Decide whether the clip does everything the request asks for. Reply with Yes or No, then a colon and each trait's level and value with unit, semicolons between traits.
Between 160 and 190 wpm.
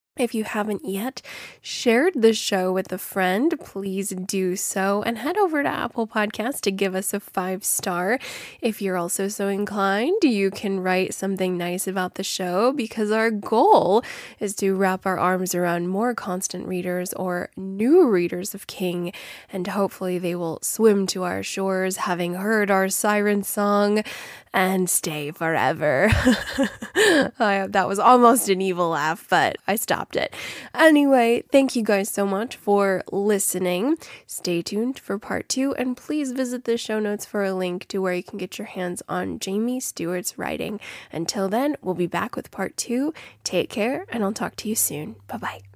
Yes: average, 175 wpm